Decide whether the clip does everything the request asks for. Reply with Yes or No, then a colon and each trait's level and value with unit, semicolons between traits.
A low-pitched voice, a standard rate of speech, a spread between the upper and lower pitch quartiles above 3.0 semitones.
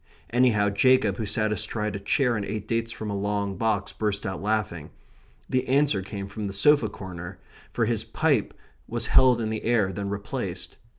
No: low, 105 Hz; average, 185 wpm; narrow, 2.5 semitones